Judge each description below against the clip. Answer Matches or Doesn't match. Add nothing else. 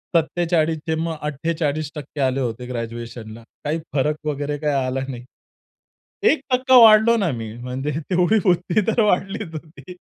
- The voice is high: Doesn't match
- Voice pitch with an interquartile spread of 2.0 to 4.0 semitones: Doesn't match